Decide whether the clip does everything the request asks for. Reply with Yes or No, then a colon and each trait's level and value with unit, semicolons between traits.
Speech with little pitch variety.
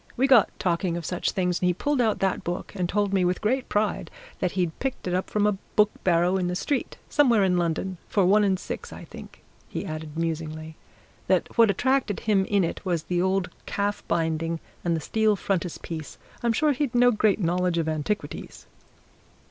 No: average, 3.7 semitones